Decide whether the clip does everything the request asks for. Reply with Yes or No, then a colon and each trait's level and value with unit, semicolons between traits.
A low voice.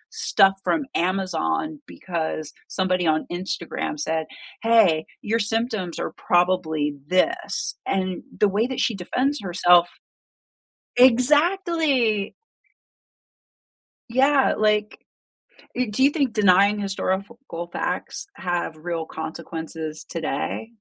No: high, 195 Hz